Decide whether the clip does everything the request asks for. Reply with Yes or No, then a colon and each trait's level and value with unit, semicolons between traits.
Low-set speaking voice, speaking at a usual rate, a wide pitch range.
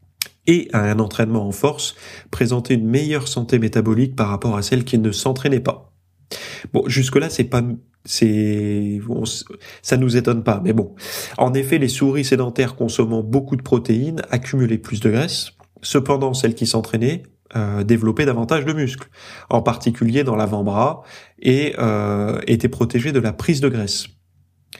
No: low, 120 Hz; average, 160 wpm; average, 3.2 semitones